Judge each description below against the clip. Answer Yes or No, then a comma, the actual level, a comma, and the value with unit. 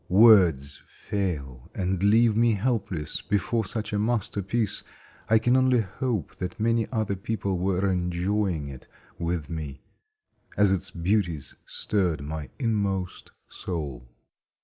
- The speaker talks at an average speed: No, slow, 125 wpm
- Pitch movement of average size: Yes, average, 4.4 semitones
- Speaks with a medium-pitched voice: No, very low, 95 Hz